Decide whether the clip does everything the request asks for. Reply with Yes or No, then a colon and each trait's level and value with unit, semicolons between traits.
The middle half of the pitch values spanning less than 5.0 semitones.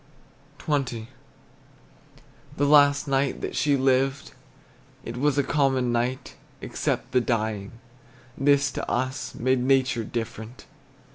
Yes: average, 2.8 semitones